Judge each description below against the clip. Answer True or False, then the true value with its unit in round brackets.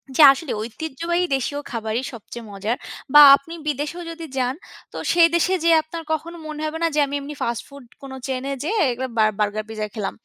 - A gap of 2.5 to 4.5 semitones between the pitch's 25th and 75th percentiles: False (5.5 semitones)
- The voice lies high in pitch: True (280 Hz)